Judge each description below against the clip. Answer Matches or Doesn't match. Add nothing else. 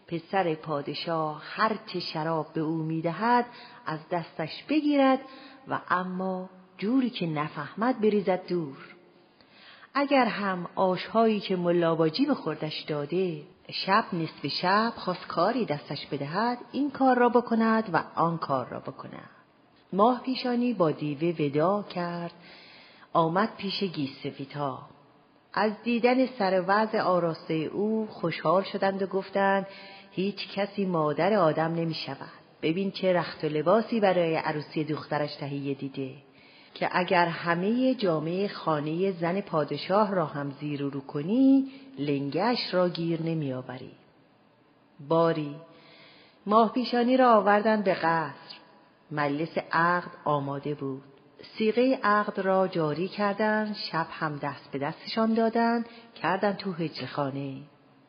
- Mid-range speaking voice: Matches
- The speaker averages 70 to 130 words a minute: Matches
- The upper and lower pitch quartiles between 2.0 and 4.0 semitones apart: Doesn't match